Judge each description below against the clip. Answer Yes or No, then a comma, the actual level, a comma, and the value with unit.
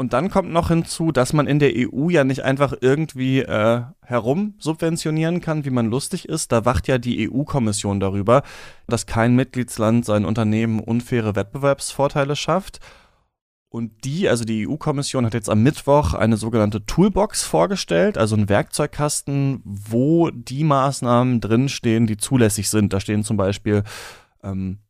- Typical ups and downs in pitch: Yes, average, 4.7 semitones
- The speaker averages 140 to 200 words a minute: Yes, average, 155 wpm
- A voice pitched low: Yes, low, 125 Hz